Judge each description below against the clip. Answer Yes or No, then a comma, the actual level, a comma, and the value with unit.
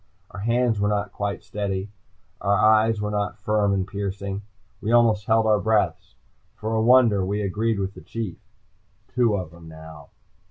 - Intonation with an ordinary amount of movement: No, narrow, 1.9 semitones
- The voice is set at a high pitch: No, low, 105 Hz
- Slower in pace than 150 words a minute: No, average, 170 wpm